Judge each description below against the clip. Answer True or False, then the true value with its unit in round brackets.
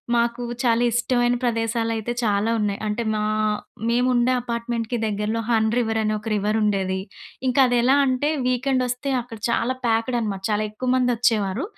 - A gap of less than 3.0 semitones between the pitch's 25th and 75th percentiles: True (2.4 semitones)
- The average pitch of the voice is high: True (230 Hz)